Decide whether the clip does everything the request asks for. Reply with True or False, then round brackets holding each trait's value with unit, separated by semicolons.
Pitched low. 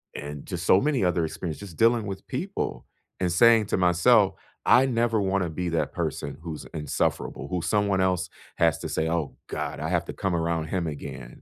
True (90 Hz)